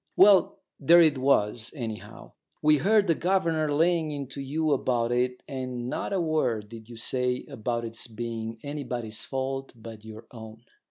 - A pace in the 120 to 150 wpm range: No, average, 160 wpm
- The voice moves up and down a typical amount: Yes, average, 4.8 semitones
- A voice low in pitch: Yes, low, 130 Hz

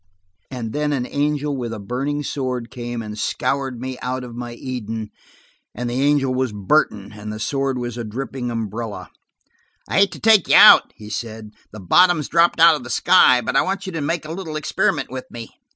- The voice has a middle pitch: No, low, 125 Hz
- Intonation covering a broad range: No, average, 4.4 semitones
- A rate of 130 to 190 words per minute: No, fast, 205 wpm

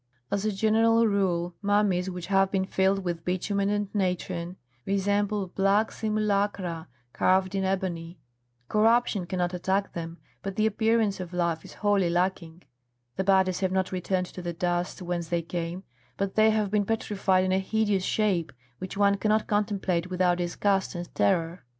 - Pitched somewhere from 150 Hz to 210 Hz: Yes, high, 190 Hz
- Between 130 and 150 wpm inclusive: No, average, 160 wpm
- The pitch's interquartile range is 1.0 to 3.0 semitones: Yes, narrow, 2.4 semitones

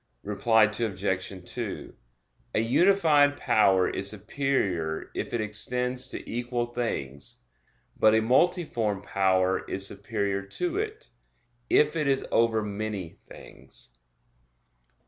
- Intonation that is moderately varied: Yes, average, 4.8 semitones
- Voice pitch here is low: Yes, low, 110 Hz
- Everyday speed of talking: No, slow, 110 wpm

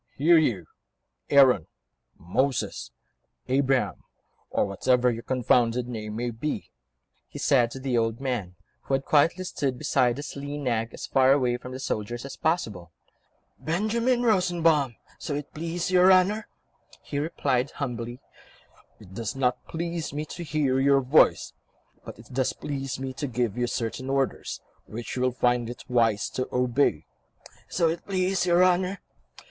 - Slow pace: No, average, 155 wpm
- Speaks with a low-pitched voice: Yes, low, 130 Hz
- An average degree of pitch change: Yes, average, 4.4 semitones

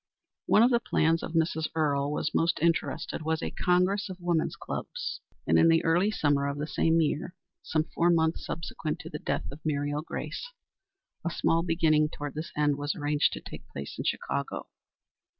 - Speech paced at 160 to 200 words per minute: Yes, average, 190 wpm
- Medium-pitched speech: Yes, medium, 160 Hz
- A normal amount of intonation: No, narrow, 2.3 semitones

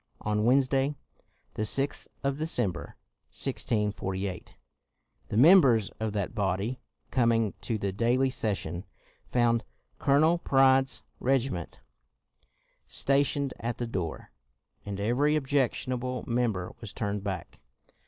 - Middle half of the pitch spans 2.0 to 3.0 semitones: No, average, 4.6 semitones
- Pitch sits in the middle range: No, low, 120 Hz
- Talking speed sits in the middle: No, slow, 115 wpm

